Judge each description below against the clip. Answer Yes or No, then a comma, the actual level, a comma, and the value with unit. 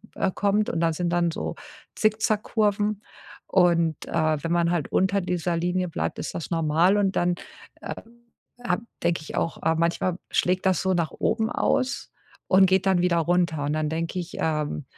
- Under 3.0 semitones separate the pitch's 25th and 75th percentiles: Yes, narrow, 2.4 semitones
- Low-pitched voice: No, medium, 175 Hz